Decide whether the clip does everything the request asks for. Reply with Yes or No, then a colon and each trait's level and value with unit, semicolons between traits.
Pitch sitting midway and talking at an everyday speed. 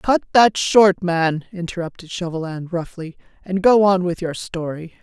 Yes: medium, 180 Hz; average, 155 wpm